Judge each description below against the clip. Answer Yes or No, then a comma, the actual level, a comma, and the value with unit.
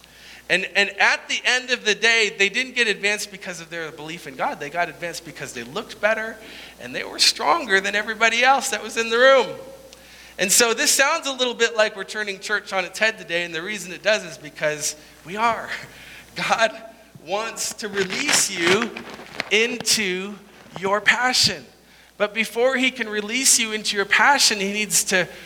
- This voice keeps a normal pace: Yes, average, 190 wpm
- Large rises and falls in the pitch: No, average, 3.4 semitones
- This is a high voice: Yes, high, 210 Hz